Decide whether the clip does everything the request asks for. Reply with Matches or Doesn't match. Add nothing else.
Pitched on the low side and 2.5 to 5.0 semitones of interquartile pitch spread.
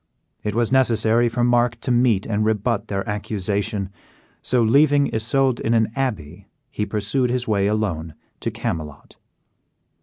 Matches